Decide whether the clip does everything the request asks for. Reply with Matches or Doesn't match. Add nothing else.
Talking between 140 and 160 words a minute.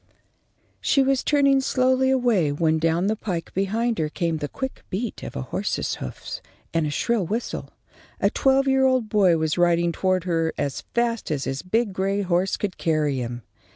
Doesn't match